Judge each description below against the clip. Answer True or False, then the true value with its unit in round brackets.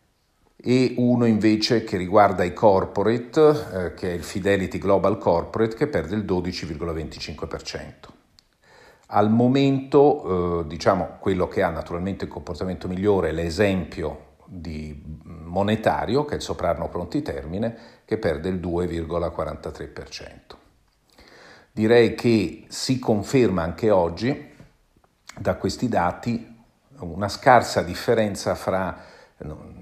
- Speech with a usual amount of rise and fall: True (4.8 semitones)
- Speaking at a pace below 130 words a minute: True (115 wpm)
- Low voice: True (100 Hz)